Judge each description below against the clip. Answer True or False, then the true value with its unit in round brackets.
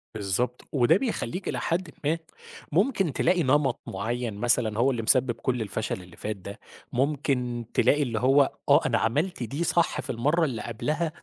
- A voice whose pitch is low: True (130 Hz)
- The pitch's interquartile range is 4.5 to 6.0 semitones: True (5.0 semitones)